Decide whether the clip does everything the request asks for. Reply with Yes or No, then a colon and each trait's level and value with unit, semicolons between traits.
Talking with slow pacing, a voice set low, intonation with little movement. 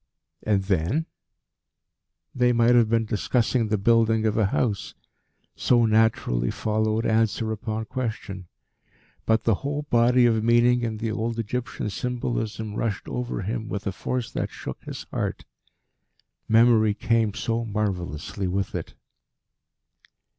Yes: slow, 130 wpm; low, 110 Hz; narrow, 1.9 semitones